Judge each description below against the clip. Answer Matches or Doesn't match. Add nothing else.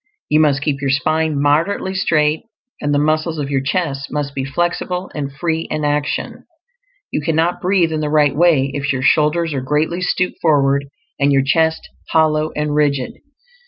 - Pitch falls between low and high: Matches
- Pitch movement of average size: Doesn't match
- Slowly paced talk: Doesn't match